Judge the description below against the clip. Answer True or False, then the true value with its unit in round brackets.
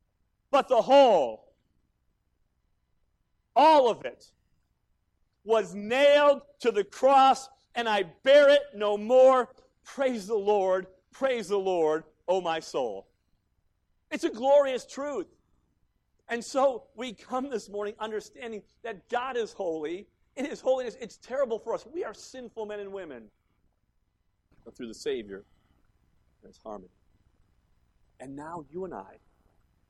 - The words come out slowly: True (130 wpm)